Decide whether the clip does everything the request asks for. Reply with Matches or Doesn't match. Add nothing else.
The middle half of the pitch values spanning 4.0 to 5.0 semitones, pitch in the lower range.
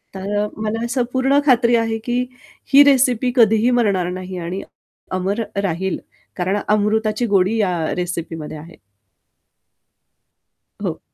Doesn't match